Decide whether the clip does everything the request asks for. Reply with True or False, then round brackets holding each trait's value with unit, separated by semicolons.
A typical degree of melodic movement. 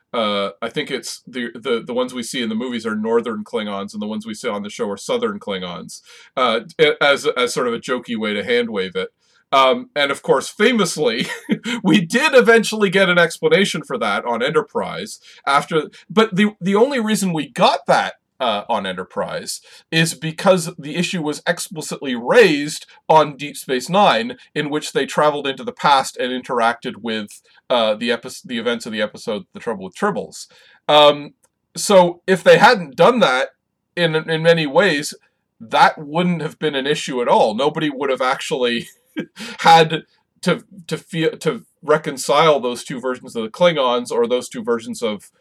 False (7.8 semitones)